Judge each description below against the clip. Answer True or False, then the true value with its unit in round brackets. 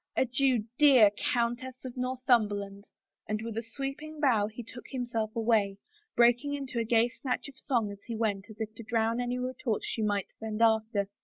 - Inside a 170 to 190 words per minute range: True (180 wpm)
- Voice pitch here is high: True (230 Hz)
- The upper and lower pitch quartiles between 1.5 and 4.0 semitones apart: True (2.8 semitones)